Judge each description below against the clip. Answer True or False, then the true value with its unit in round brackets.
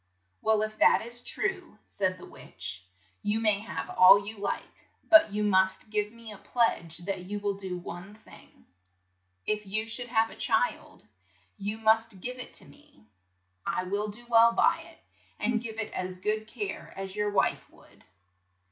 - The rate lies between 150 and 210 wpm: True (175 wpm)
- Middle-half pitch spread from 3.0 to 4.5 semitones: False (2.6 semitones)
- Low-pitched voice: False (210 Hz)